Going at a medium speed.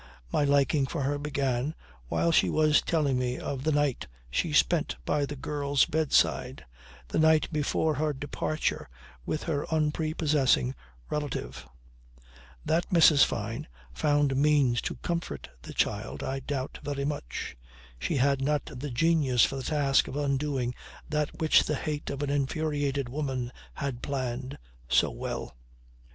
Yes: average, 150 wpm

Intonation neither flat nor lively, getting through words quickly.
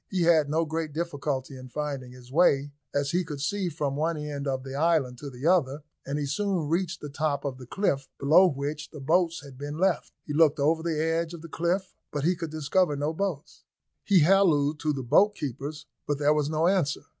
Yes: average, 3.1 semitones; fast, 220 wpm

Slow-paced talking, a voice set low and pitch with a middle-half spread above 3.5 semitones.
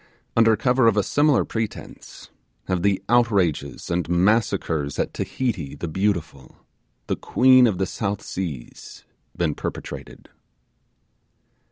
Yes: slow, 120 wpm; low, 100 Hz; average, 5.1 semitones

